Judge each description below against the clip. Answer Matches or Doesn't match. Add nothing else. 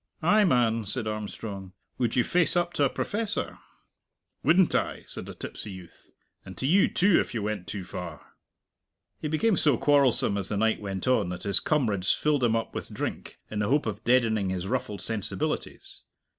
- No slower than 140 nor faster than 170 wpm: Doesn't match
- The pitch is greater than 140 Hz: Doesn't match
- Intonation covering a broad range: Matches